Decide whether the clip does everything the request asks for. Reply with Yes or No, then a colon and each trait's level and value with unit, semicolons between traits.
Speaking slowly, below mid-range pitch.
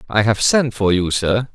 No: fast, 235 wpm; low, 110 Hz